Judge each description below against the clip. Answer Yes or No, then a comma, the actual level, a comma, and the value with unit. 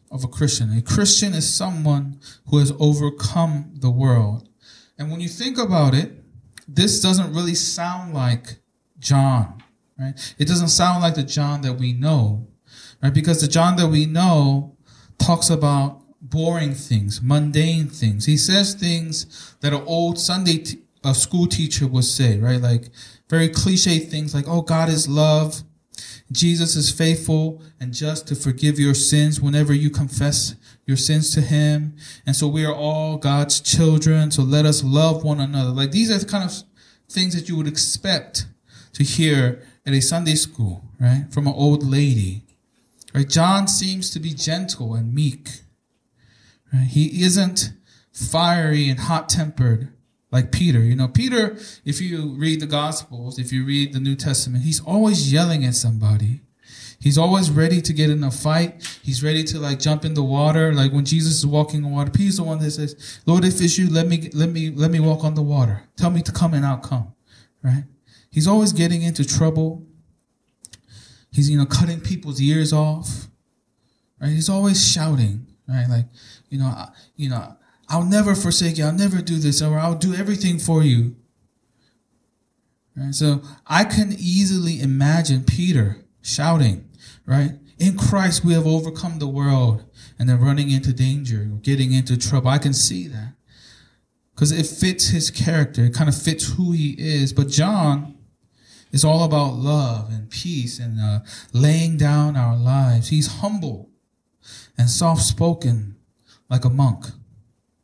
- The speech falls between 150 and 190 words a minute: Yes, average, 170 wpm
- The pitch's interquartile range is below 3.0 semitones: No, average, 4.3 semitones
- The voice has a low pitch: No, medium, 145 Hz